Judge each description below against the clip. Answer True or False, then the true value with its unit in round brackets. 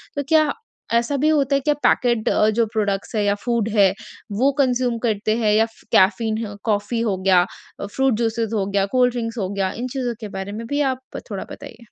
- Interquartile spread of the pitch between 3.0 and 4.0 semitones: True (3.6 semitones)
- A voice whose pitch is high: True (225 Hz)